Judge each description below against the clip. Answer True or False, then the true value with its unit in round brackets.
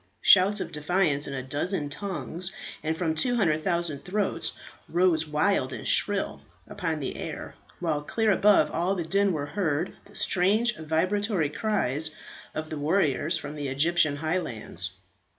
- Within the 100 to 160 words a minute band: True (145 wpm)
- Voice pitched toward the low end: False (165 Hz)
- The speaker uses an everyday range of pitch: True (4.5 semitones)